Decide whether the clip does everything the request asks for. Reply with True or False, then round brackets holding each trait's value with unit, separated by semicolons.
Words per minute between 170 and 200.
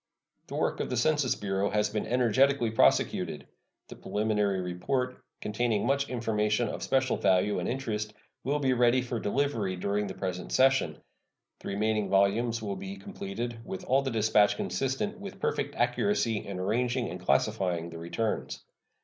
False (160 wpm)